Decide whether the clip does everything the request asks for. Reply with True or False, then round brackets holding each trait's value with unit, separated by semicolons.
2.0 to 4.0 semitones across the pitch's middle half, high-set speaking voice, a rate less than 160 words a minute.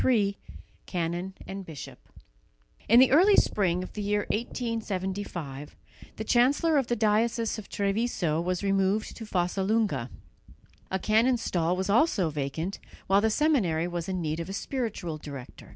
False (4.6 semitones; 195 Hz; 150 wpm)